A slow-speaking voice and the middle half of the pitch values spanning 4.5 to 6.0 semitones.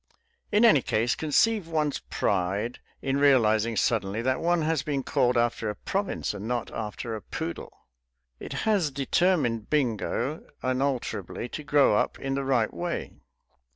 No: average, 150 wpm; average, 5.0 semitones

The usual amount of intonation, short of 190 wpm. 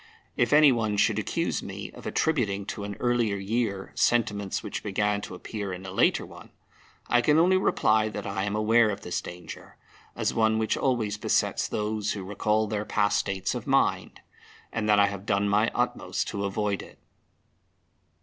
No: narrow, 1.9 semitones; average, 180 wpm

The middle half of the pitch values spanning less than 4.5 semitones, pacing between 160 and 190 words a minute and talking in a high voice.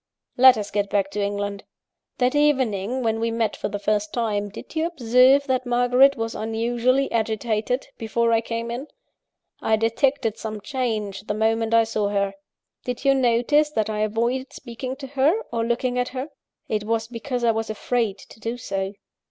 Yes: average, 3.0 semitones; average, 180 wpm; high, 230 Hz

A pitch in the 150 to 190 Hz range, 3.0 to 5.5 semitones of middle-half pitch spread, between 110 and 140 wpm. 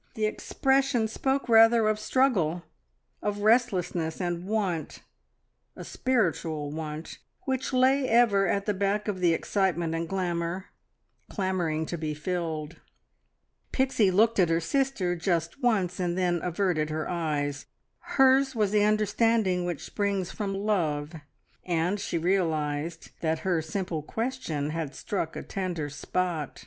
Yes: medium, 185 Hz; average, 4.6 semitones; slow, 135 wpm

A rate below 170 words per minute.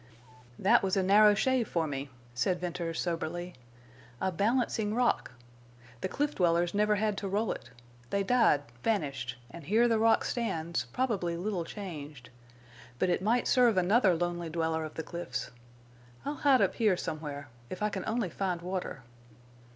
Yes: average, 160 wpm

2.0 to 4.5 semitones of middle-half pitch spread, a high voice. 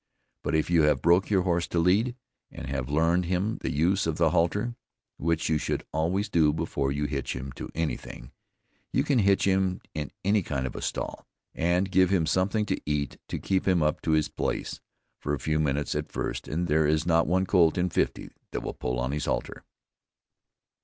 No: average, 3.8 semitones; very low, 85 Hz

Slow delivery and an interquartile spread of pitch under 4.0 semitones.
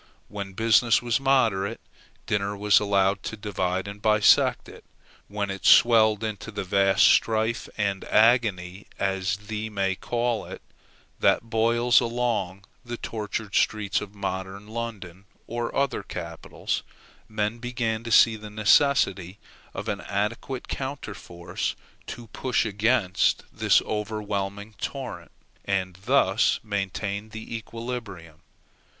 Yes: slow, 120 wpm; average, 2.8 semitones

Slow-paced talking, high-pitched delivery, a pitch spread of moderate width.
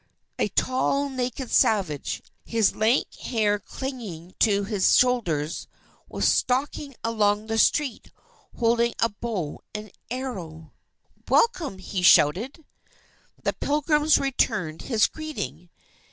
Yes: slow, 110 wpm; high, 230 Hz; average, 5.0 semitones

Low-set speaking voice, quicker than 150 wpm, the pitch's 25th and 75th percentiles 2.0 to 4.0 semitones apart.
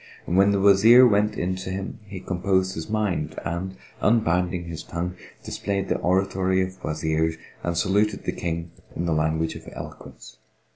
Yes: very low, 95 Hz; average, 160 wpm; narrow, 2.6 semitones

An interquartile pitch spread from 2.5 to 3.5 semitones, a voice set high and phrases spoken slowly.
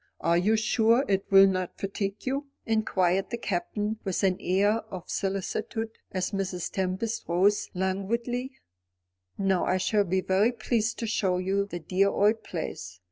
No: average, 2.8 semitones; high, 195 Hz; average, 155 wpm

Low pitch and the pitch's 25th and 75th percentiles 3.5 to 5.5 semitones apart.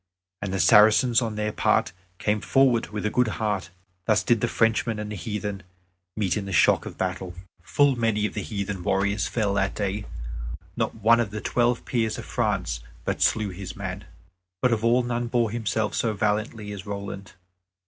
No: low, 105 Hz; narrow, 2.5 semitones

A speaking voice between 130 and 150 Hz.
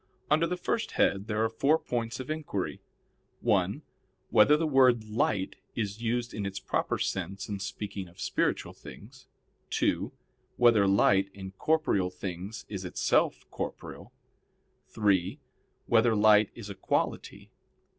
No: low, 105 Hz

